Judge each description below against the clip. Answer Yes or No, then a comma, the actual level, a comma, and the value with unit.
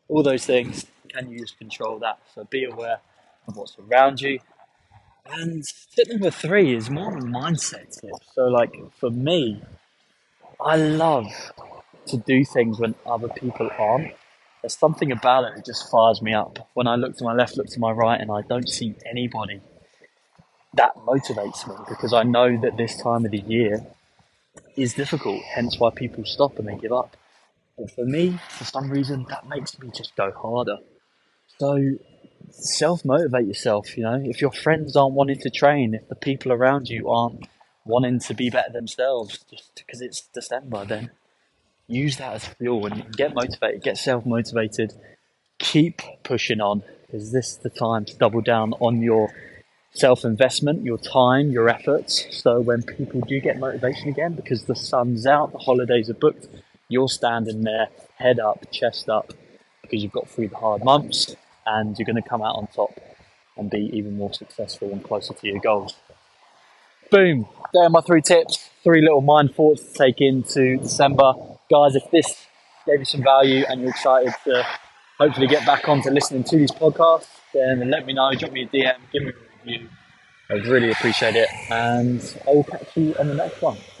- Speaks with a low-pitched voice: Yes, low, 125 Hz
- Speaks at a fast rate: No, average, 180 wpm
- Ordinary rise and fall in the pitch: Yes, average, 3.3 semitones